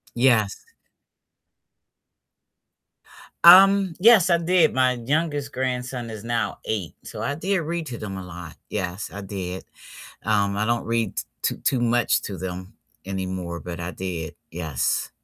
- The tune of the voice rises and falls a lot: Yes, wide, 7.2 semitones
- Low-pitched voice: Yes, low, 115 Hz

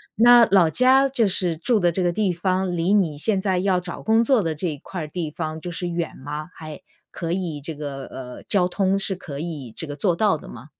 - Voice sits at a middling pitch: Yes, medium, 175 Hz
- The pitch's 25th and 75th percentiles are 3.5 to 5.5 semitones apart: Yes, average, 3.9 semitones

